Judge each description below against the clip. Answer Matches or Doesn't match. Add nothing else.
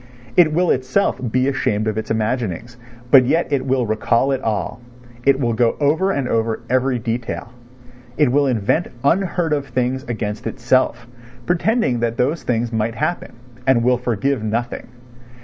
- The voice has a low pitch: Matches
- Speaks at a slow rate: Doesn't match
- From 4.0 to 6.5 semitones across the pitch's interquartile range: Doesn't match